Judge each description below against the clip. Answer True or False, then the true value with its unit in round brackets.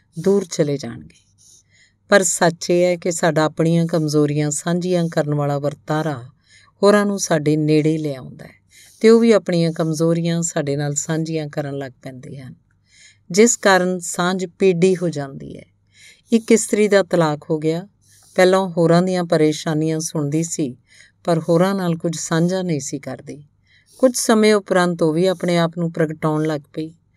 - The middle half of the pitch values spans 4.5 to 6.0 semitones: False (3.5 semitones)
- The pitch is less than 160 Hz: False (165 Hz)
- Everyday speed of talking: True (155 wpm)